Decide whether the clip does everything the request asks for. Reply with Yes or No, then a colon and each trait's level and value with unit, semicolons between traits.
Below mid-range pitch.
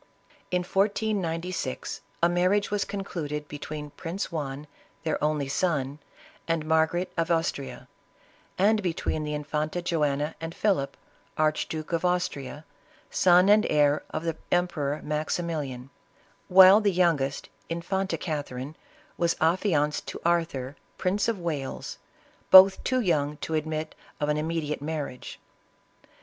No: medium, 160 Hz